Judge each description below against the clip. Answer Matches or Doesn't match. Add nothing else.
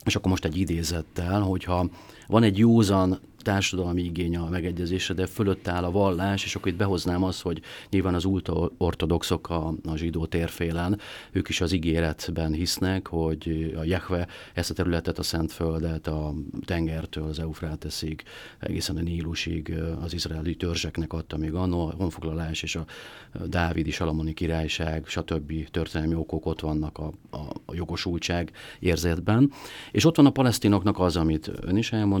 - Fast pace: Matches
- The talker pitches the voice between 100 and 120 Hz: Doesn't match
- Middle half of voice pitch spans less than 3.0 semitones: Matches